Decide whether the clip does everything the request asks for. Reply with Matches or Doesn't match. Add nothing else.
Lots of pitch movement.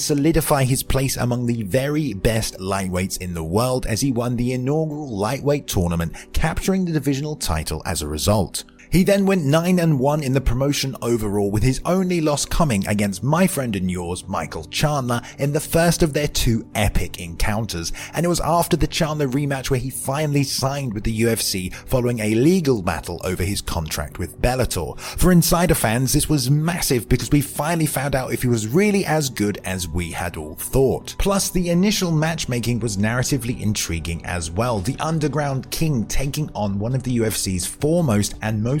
Matches